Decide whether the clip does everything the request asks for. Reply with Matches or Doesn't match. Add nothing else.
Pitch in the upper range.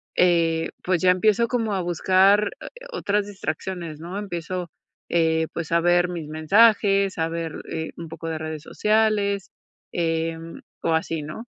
Doesn't match